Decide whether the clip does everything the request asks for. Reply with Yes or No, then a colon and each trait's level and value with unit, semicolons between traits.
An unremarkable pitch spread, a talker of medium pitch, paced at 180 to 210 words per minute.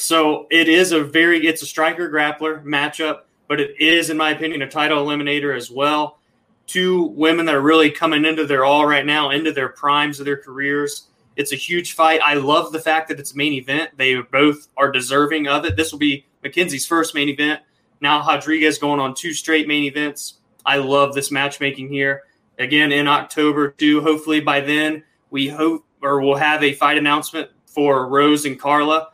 No: narrow, 1.9 semitones; medium, 150 Hz; average, 200 wpm